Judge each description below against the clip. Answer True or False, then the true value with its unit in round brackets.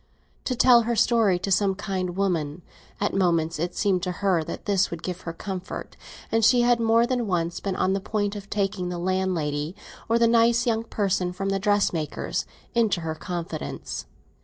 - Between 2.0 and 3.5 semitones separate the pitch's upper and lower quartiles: False (3.9 semitones)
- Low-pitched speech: False (195 Hz)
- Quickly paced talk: False (185 wpm)